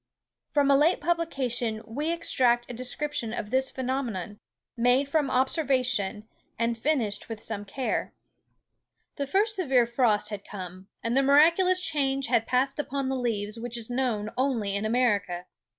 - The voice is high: Yes, very high, 250 Hz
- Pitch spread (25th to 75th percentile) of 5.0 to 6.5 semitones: No, average, 3.9 semitones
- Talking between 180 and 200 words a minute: No, average, 150 wpm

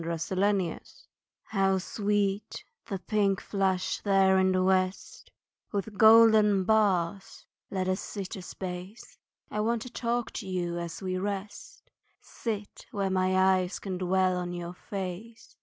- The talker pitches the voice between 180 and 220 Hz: Yes, high, 190 Hz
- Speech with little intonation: Yes, narrow, 1.9 semitones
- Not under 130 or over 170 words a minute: Yes, average, 150 wpm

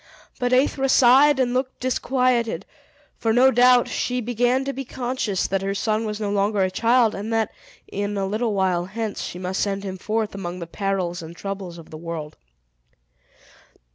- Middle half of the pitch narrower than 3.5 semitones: No, average, 4.3 semitones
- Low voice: No, high, 215 Hz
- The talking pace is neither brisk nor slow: Yes, average, 180 wpm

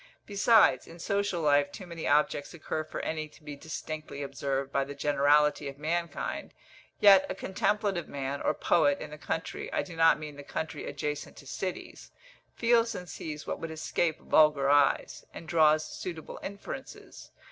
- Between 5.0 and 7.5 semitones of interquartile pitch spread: No, average, 3.2 semitones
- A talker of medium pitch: Yes, medium, 155 Hz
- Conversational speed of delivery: Yes, average, 170 wpm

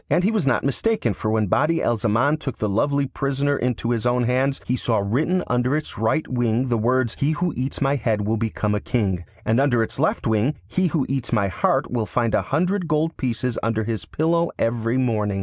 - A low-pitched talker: Yes, low, 125 Hz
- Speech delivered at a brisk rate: Yes, fast, 220 wpm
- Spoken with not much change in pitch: No, average, 4.3 semitones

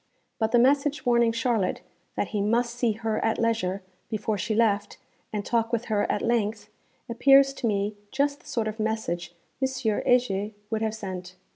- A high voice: Yes, high, 225 Hz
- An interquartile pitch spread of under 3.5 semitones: Yes, narrow, 2.4 semitones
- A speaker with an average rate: Yes, average, 175 wpm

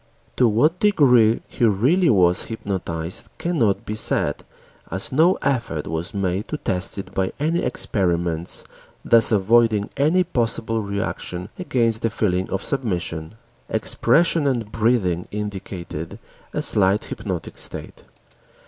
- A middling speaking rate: No, slow, 125 wpm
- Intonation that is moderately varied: Yes, average, 4.8 semitones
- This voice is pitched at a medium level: No, low, 105 Hz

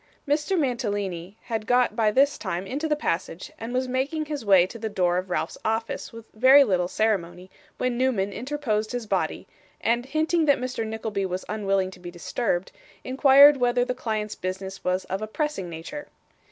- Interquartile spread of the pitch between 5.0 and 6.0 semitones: Yes, average, 5.3 semitones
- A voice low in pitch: No, high, 220 Hz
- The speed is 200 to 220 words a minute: No, average, 180 wpm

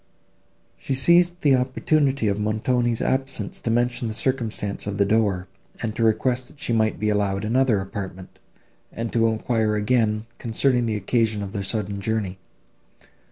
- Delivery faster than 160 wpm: No, average, 155 wpm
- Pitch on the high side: No, low, 110 Hz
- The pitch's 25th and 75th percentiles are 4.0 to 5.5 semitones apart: No, average, 3.1 semitones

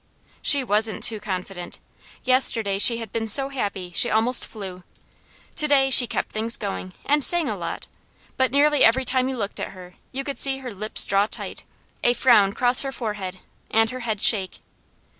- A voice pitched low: No, high, 225 Hz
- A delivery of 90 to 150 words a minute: No, average, 185 wpm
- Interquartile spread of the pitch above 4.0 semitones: Yes, average, 4.5 semitones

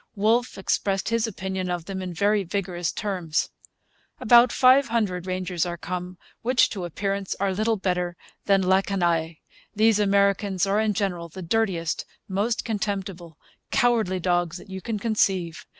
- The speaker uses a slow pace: No, average, 150 wpm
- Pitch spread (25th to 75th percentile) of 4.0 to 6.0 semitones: No, average, 3.0 semitones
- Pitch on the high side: Yes, high, 195 Hz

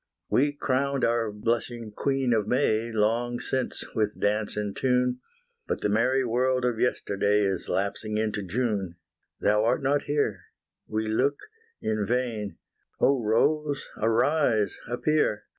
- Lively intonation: No, average, 3.4 semitones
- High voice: No, low, 115 Hz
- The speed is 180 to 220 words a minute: No, slow, 135 wpm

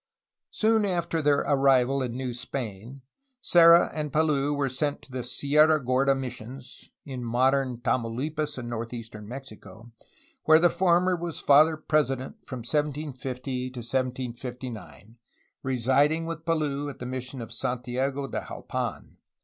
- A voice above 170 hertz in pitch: No, low, 135 Hz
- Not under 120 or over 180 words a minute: Yes, slow, 135 wpm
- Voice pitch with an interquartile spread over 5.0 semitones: No, average, 3.3 semitones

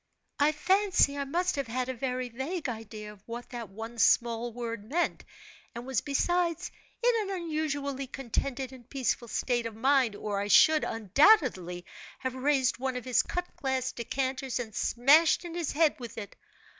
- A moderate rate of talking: Yes, average, 170 wpm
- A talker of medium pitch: No, very high, 260 Hz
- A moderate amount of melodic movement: Yes, average, 4.1 semitones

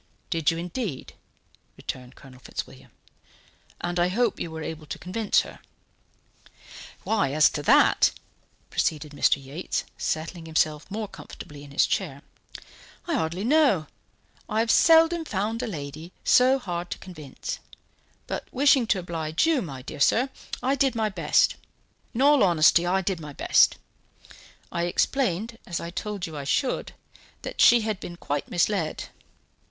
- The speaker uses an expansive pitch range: Yes, wide, 6.4 semitones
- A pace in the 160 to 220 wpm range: No, average, 150 wpm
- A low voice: No, medium, 175 Hz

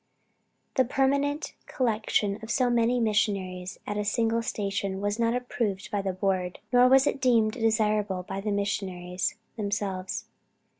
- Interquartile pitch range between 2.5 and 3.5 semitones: Yes, average, 3.1 semitones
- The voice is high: Yes, high, 210 Hz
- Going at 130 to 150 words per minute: Yes, average, 145 wpm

